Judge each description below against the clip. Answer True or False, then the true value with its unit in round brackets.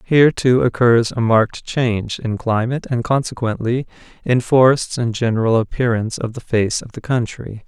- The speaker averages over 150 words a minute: True (165 wpm)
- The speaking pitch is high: False (120 Hz)